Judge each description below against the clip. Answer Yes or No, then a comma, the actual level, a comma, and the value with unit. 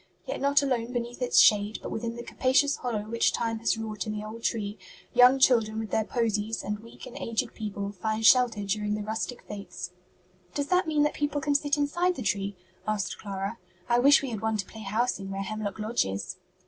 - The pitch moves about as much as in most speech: Yes, average, 3.1 semitones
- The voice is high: Yes, high, 225 Hz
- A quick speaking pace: Yes, fast, 215 wpm